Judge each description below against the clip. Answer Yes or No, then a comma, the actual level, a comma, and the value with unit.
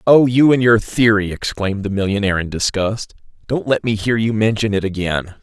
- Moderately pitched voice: No, low, 105 Hz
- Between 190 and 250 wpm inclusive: Yes, average, 200 wpm